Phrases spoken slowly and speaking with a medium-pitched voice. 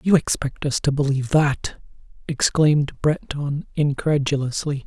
Yes: slow, 110 wpm; medium, 145 Hz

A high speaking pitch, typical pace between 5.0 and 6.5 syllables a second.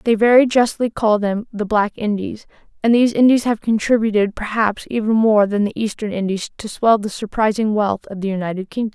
Yes: high, 215 Hz; 5.5 syllables/s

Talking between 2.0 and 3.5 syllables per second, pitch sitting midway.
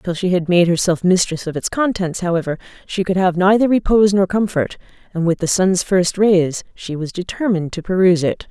No: 5.6 syllables/s; medium, 180 Hz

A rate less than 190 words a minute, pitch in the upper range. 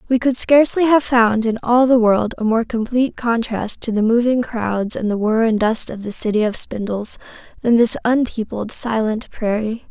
No: average, 195 wpm; high, 230 Hz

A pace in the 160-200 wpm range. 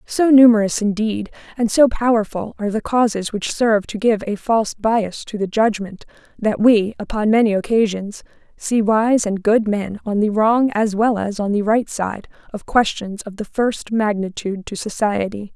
Yes: average, 180 wpm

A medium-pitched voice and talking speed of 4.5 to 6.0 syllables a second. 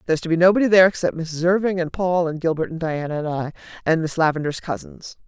No: medium, 165 Hz; 6.6 syllables/s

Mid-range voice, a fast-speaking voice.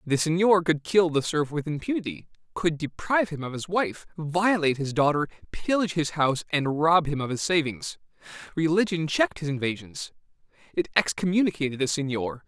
No: medium, 160 Hz; average, 165 wpm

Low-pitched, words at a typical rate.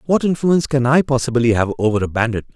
No: low, 130 Hz; fast, 210 wpm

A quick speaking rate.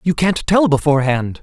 No: average, 170 wpm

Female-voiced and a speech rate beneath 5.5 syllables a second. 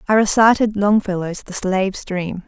Yes: female; 4.8 syllables/s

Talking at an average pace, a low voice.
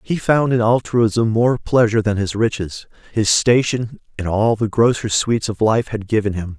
Yes: average, 190 wpm; low, 110 Hz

